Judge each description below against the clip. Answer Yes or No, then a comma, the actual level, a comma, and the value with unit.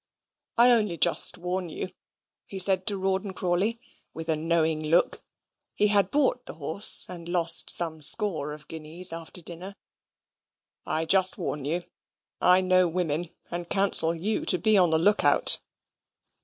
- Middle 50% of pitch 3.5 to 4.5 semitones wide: No, average, 2.9 semitones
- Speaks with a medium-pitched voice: Yes, medium, 175 Hz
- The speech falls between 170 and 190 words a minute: No, average, 155 wpm